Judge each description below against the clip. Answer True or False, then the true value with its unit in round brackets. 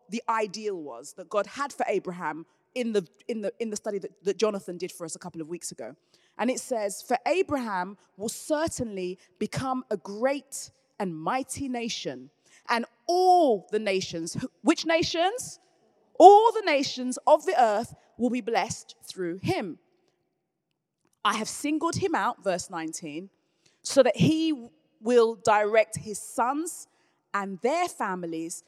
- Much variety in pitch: True (6.2 semitones)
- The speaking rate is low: False (155 wpm)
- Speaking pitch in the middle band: False (215 Hz)